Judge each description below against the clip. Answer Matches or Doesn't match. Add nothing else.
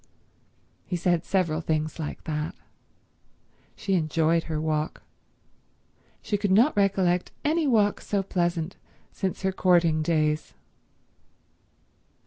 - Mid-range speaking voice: Matches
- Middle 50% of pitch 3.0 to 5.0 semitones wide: Matches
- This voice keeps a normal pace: Doesn't match